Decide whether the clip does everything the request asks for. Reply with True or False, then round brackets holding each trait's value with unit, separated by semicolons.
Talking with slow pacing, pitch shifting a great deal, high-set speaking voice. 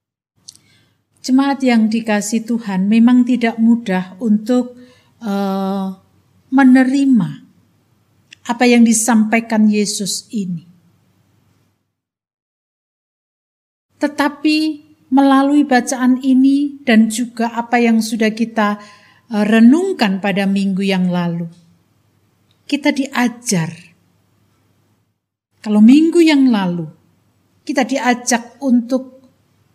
True (80 wpm; 5.8 semitones; 225 Hz)